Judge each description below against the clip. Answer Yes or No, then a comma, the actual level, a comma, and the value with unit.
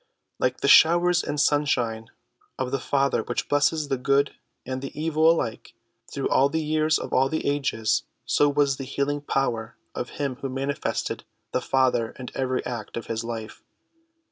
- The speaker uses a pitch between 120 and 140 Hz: Yes, low, 135 Hz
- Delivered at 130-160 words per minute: No, average, 170 wpm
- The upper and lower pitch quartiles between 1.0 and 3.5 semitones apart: Yes, narrow, 2.5 semitones